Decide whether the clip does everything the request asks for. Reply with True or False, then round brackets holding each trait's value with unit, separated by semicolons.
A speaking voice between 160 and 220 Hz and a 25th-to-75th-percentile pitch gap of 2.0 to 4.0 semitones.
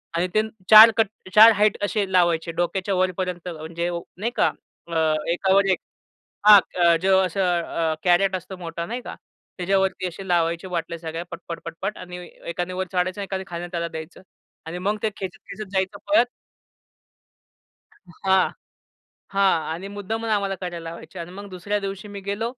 True (185 Hz; 2.5 semitones)